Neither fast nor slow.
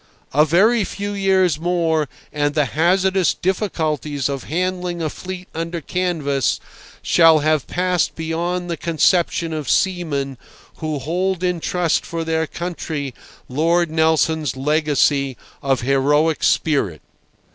No: slow, 125 wpm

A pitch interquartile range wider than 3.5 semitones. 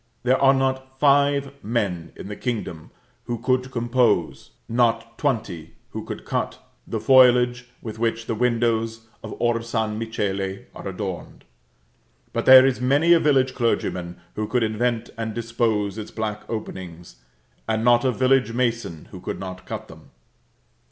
No: average, 3.0 semitones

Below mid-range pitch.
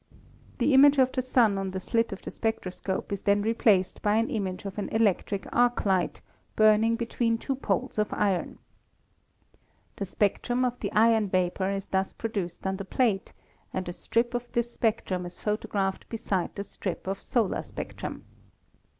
No: high, 210 Hz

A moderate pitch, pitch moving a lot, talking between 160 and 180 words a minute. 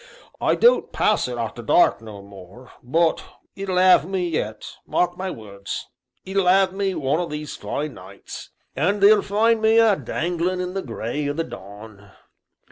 Yes: medium, 165 Hz; wide, 8.9 semitones; average, 170 wpm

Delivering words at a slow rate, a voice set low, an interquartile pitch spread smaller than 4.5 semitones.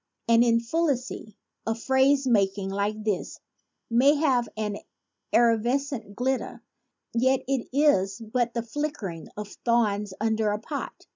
No: slow, 120 wpm; high, 230 Hz; average, 3.9 semitones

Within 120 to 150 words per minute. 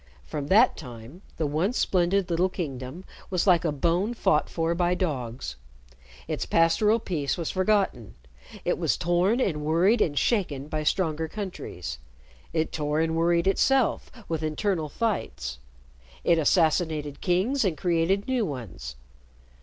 Yes: average, 140 wpm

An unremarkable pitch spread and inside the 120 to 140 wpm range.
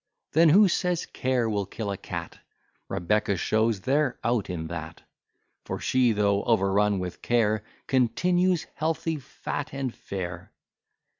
No: wide, 6.3 semitones; slow, 135 wpm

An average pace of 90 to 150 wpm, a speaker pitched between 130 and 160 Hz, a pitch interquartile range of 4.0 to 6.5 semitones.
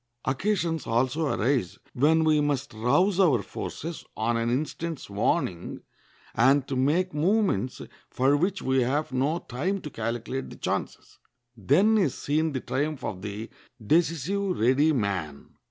Yes: average, 140 wpm; medium, 140 Hz; wide, 5.4 semitones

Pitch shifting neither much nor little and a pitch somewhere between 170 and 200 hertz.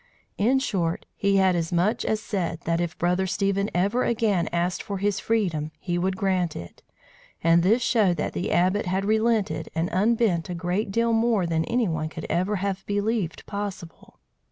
Yes: average, 3.5 semitones; high, 190 Hz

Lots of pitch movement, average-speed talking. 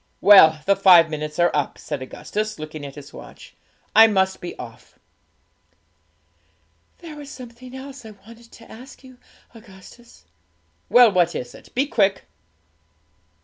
Yes: wide, 6.7 semitones; average, 145 wpm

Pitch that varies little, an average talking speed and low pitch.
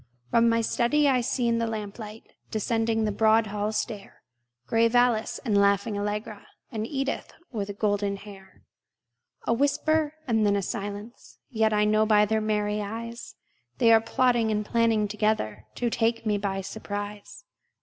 No: narrow, 2.0 semitones; average, 160 wpm; high, 220 Hz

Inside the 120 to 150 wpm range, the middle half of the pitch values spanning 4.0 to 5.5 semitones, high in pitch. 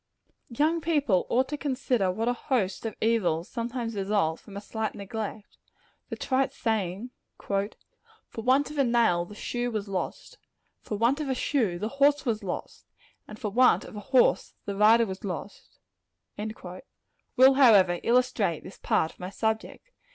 No: average, 165 wpm; average, 4.3 semitones; high, 220 Hz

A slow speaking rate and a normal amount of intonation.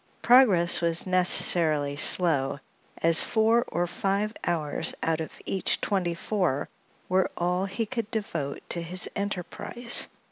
Yes: slow, 130 wpm; average, 3.7 semitones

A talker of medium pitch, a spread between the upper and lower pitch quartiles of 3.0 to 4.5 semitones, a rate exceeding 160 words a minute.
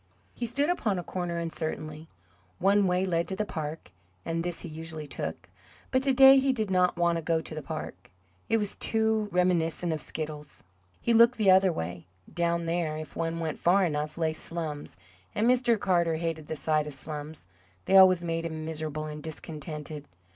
Yes: medium, 165 Hz; average, 3.5 semitones; average, 190 wpm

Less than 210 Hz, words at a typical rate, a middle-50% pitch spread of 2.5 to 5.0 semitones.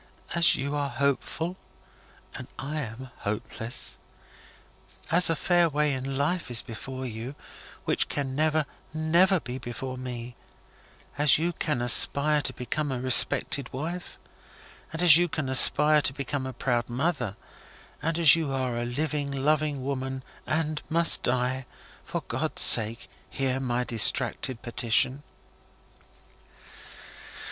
No: low, 135 Hz; slow, 130 wpm; average, 3.5 semitones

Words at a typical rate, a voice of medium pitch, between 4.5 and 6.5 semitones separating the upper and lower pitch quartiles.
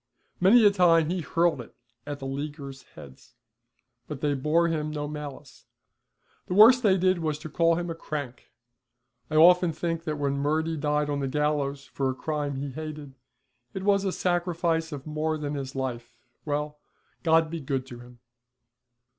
No: average, 175 wpm; medium, 150 Hz; average, 3.0 semitones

